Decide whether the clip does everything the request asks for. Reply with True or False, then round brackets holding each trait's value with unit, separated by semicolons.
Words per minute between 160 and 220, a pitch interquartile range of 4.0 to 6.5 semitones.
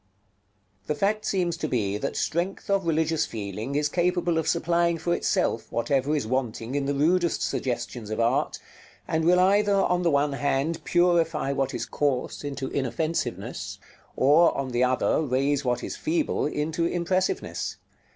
True (165 wpm; 4.5 semitones)